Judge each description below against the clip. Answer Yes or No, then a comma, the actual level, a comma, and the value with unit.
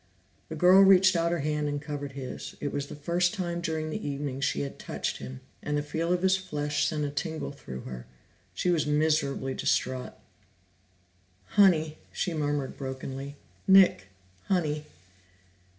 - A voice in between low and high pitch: Yes, medium, 150 Hz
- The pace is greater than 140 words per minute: Yes, average, 165 wpm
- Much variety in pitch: No, average, 3.4 semitones